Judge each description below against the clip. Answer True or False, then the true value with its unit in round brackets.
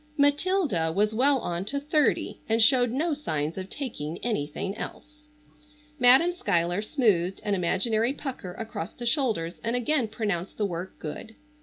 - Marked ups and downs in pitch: True (7.4 semitones)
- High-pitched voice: True (225 Hz)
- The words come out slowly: False (150 wpm)